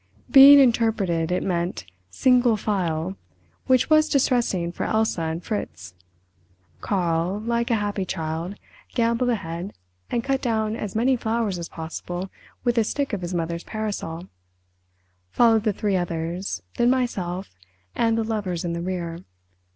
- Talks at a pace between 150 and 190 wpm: No, slow, 135 wpm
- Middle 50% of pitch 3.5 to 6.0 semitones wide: Yes, wide, 5.6 semitones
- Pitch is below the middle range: No, high, 190 Hz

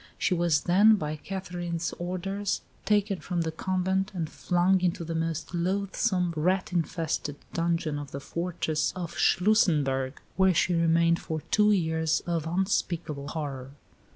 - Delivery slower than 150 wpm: Yes, average, 140 wpm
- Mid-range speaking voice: Yes, medium, 170 Hz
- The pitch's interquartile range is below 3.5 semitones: Yes, average, 2.7 semitones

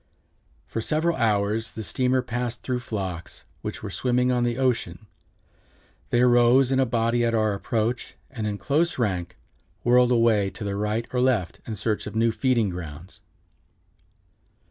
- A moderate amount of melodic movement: Yes, average, 3.0 semitones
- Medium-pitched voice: No, low, 115 Hz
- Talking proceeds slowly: No, average, 160 wpm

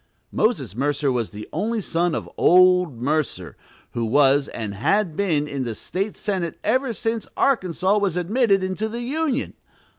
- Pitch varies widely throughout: Yes, wide, 6.9 semitones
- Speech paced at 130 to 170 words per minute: Yes, average, 155 wpm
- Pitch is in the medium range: Yes, medium, 180 Hz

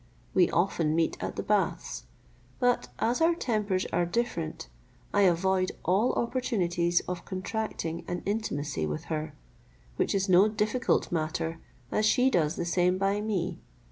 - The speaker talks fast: No, average, 145 wpm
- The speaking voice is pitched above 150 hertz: Yes, medium, 185 Hz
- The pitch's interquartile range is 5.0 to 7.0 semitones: No, average, 4.1 semitones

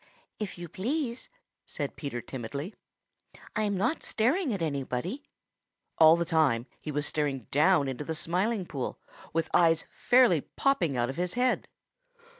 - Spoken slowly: No, average, 145 wpm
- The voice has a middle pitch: Yes, medium, 165 Hz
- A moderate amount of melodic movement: No, wide, 7.2 semitones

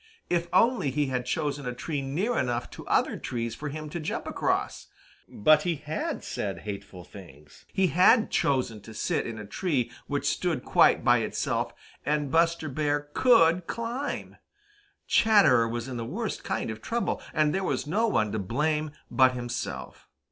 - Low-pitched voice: No, medium, 145 Hz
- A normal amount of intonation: No, wide, 6.0 semitones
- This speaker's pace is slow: No, average, 170 wpm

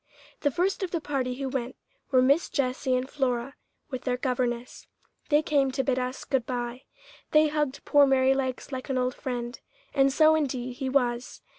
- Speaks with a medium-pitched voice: No, very high, 260 Hz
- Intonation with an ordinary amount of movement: No, narrow, 2.0 semitones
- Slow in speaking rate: No, average, 180 wpm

